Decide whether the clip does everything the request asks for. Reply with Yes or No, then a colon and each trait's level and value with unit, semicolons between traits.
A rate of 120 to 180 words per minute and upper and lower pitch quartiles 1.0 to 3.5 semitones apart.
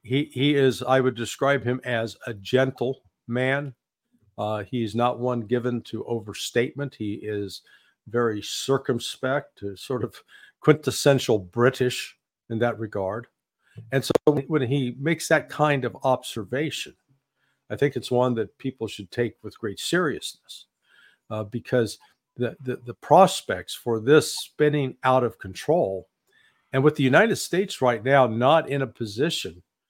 Yes: average, 145 wpm; average, 3.2 semitones